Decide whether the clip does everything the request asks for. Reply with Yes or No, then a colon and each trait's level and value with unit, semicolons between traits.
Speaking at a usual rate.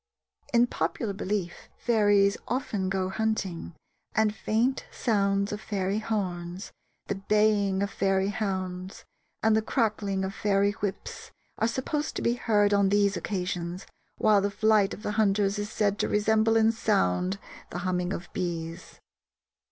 Yes: average, 145 wpm